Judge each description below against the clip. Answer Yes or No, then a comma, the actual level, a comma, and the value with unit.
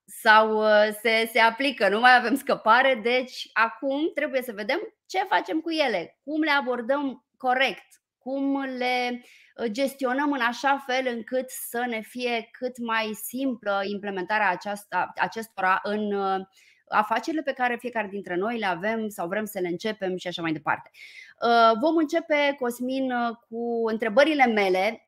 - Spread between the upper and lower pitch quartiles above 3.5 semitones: Yes, average, 3.9 semitones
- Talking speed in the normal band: Yes, average, 145 wpm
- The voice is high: Yes, high, 235 Hz